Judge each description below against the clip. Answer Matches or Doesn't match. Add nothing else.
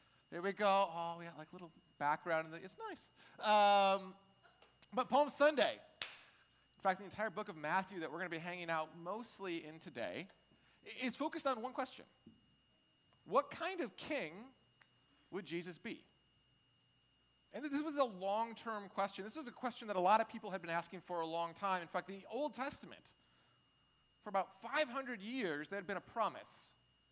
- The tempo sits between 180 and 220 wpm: Matches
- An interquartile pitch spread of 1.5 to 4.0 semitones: Doesn't match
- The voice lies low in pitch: Doesn't match